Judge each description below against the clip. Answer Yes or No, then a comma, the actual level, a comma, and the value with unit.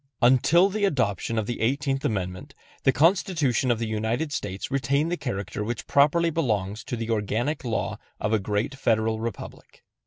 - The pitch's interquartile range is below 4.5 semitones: No, average, 4.8 semitones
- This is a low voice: Yes, low, 120 Hz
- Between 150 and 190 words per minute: Yes, average, 165 wpm